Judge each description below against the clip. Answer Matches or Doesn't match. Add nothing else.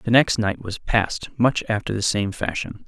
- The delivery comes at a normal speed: Doesn't match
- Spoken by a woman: Doesn't match